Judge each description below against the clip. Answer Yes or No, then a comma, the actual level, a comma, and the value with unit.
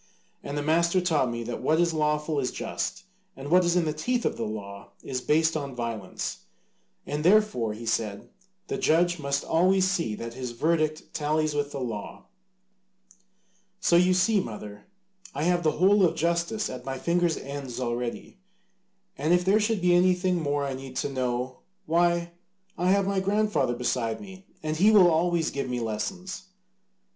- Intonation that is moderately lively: No, wide, 5.7 semitones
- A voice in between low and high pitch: Yes, medium, 155 Hz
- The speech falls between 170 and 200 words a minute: Yes, average, 175 wpm